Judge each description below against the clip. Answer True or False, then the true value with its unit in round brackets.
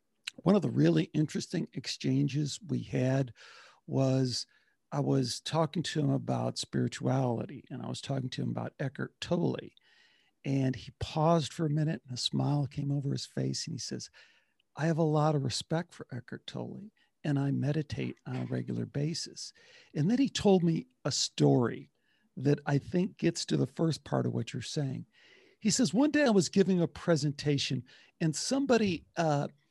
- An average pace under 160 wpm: False (180 wpm)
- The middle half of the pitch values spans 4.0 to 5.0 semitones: True (4.3 semitones)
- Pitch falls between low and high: True (145 Hz)